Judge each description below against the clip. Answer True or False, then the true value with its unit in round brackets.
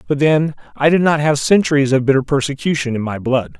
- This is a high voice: False (140 Hz)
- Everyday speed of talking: False (215 wpm)